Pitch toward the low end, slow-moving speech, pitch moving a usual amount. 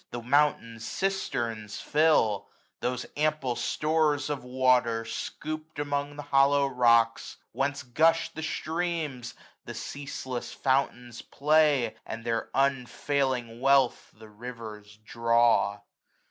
Yes: low, 130 Hz; slow, 110 wpm; average, 3.9 semitones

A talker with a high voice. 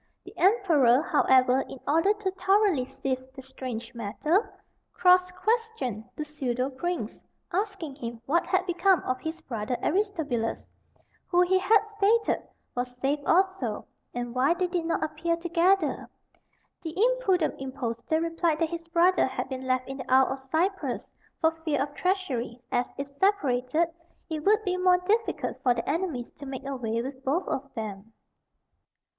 Yes: very high, 310 Hz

